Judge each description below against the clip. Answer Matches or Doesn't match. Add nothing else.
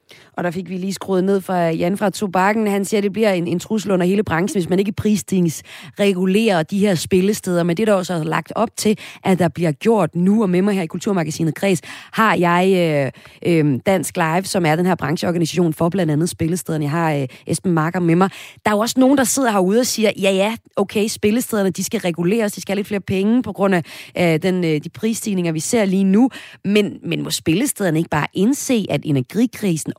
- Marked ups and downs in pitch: Doesn't match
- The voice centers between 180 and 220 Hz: Matches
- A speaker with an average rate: Doesn't match